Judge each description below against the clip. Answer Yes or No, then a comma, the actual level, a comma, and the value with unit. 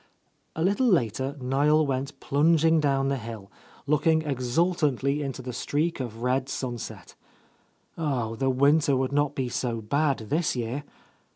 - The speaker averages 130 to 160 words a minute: Yes, average, 150 wpm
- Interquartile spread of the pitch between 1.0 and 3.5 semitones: Yes, average, 3.2 semitones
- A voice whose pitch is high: No, medium, 140 Hz